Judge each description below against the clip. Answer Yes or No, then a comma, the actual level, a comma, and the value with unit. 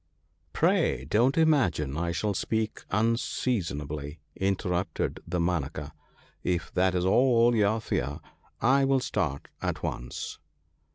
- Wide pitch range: Yes, wide, 6.7 semitones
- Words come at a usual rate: No, slow, 120 wpm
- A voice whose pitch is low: Yes, very low, 95 Hz